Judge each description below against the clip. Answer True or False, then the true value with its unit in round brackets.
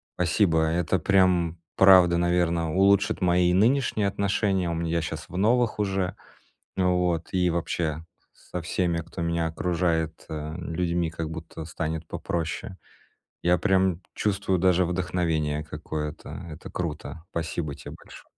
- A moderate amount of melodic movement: False (2.3 semitones)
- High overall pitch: False (85 Hz)